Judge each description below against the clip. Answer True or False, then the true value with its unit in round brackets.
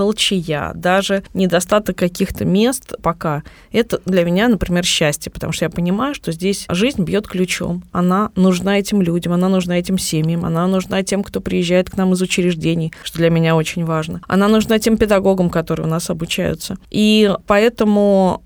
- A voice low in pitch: False (185 Hz)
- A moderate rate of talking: False (170 wpm)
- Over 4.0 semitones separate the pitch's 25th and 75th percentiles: False (2.7 semitones)